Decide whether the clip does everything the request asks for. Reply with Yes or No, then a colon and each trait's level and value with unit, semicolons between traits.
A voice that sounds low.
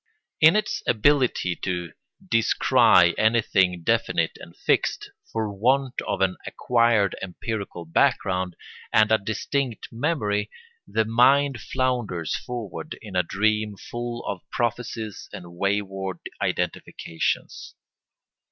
Yes: low, 110 Hz